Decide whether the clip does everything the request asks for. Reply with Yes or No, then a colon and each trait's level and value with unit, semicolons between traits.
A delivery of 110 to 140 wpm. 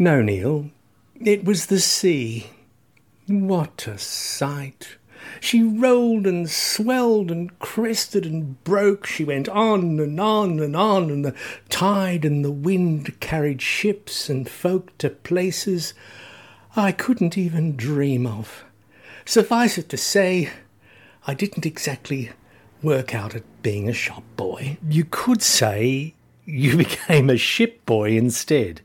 Yes: slow, 135 wpm